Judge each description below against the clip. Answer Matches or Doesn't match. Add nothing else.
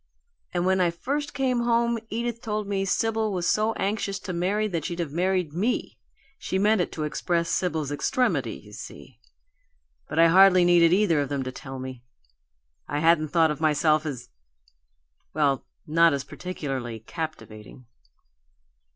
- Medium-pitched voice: Matches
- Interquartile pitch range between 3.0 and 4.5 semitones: Doesn't match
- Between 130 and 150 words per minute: Doesn't match